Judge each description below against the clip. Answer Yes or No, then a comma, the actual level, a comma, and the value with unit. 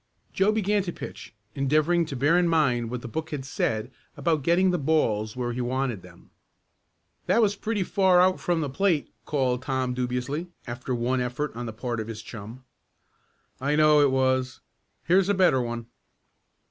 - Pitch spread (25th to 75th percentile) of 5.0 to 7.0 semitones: Yes, wide, 5.6 semitones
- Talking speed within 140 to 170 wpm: No, average, 180 wpm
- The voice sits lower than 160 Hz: Yes, low, 135 Hz